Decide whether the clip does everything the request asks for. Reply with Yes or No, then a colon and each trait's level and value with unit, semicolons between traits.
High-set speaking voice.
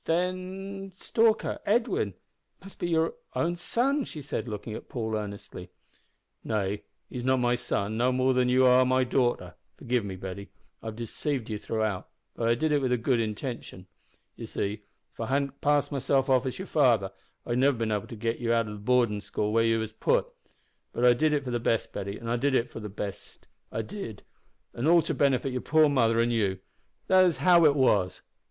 No: low, 125 Hz